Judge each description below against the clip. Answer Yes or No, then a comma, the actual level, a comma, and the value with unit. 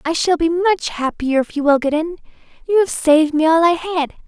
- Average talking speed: No, fast, 240 wpm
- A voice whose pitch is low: No, very high, 320 Hz